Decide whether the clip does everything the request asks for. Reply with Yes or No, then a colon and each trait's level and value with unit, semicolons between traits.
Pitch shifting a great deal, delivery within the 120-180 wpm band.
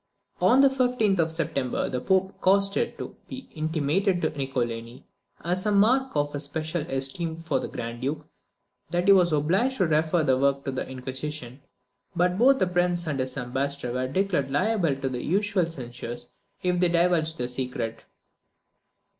Yes: wide, 5.7 semitones; average, 170 wpm